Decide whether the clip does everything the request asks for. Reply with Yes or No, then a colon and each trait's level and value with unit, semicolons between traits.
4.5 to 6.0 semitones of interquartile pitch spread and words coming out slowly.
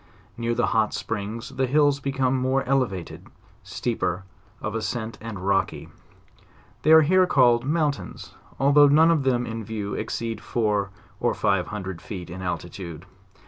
No: average, 5.2 semitones; average, 150 wpm